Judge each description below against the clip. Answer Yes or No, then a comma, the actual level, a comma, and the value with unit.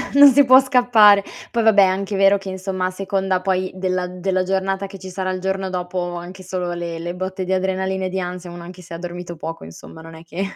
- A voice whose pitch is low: No, medium, 185 Hz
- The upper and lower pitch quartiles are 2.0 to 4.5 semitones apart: No, narrow, 1.4 semitones